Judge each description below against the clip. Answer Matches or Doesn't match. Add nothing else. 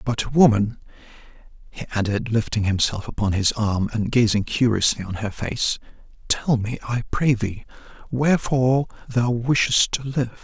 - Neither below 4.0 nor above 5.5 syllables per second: Matches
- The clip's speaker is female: Doesn't match